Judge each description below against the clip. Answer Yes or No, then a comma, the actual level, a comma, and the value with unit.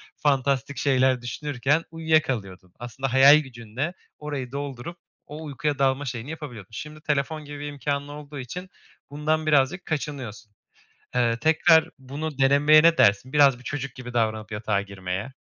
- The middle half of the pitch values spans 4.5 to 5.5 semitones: No, average, 3.6 semitones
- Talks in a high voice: No, medium, 140 Hz